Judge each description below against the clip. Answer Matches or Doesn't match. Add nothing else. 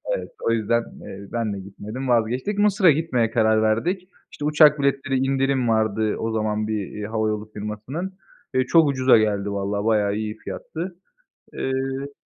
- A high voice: Doesn't match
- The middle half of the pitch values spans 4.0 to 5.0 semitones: Matches